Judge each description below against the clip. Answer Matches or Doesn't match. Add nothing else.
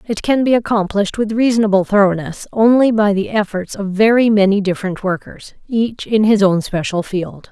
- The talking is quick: Doesn't match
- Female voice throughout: Matches